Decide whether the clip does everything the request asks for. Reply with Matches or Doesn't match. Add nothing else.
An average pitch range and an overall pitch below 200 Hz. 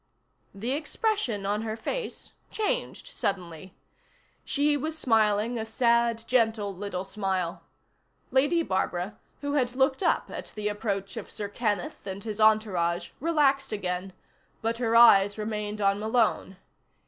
Doesn't match